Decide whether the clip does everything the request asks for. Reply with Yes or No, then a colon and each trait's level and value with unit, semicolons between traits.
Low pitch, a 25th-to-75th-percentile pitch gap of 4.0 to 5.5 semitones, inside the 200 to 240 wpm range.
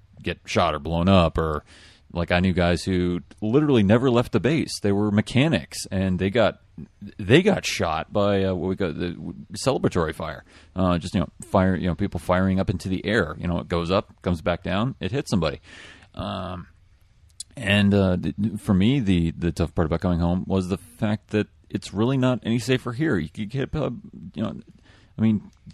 No: very low, 95 Hz; average, 3.3 semitones; fast, 205 wpm